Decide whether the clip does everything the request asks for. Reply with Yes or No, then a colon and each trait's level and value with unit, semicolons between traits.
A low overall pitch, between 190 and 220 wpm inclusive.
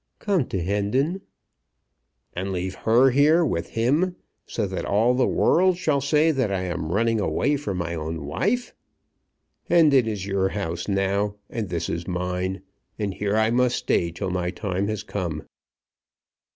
No: low, 100 Hz; average, 160 wpm